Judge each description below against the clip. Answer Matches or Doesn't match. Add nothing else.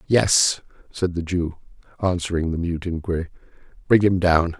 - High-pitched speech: Doesn't match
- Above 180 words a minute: Doesn't match